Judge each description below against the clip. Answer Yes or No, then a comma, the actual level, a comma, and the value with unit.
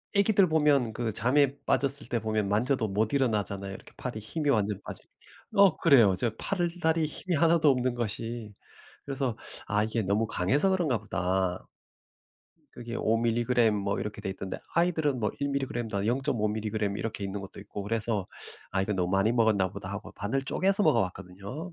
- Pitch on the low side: Yes, low, 115 Hz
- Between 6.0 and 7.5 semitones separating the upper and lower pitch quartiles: No, wide, 5.4 semitones